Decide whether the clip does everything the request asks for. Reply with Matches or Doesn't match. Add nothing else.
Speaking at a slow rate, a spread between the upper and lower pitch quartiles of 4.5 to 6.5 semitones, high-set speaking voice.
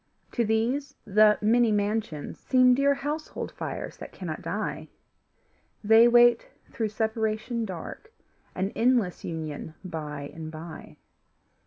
Matches